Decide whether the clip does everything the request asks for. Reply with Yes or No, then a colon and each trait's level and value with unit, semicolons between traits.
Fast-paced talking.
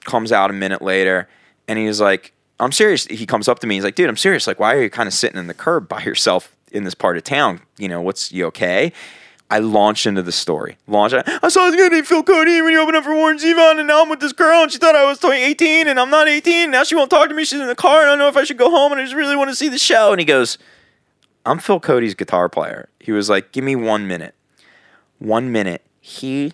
Yes: fast, 280 wpm